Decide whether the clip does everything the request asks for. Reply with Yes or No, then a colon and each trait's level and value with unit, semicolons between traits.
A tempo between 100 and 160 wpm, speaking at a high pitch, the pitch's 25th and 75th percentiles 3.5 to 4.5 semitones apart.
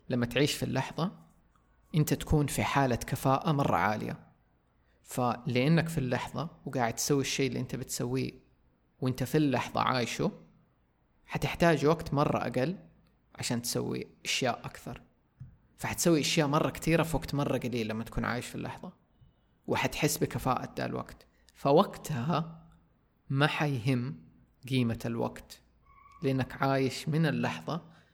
No: average, 120 wpm; low, 135 Hz; average, 3.9 semitones